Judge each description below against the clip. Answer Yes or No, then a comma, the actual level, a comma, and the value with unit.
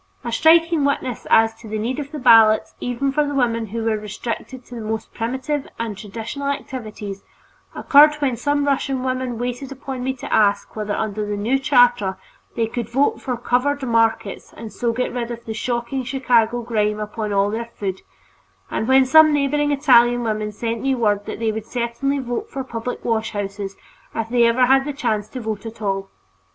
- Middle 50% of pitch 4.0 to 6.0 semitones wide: No, average, 3.4 semitones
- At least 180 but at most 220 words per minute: Yes, average, 190 wpm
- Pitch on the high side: Yes, high, 235 Hz